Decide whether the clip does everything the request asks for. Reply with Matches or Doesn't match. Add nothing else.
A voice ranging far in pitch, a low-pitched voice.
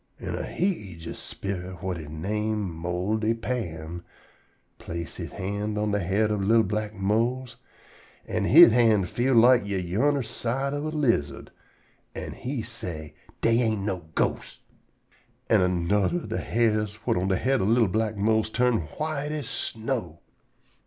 Doesn't match